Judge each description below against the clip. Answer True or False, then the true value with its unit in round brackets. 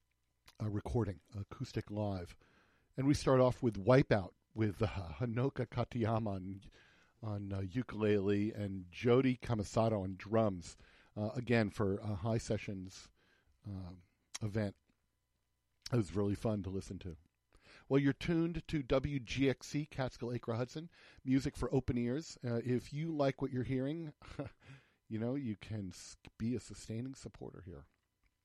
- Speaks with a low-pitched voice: True (110 Hz)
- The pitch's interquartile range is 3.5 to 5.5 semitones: True (4.2 semitones)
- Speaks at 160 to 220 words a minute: False (140 wpm)